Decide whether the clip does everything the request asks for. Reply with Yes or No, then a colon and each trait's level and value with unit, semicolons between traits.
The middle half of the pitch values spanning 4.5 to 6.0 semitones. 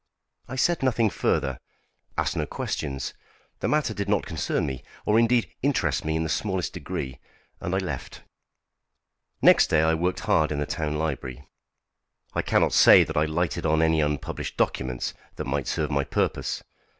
Yes: wide, 5.6 semitones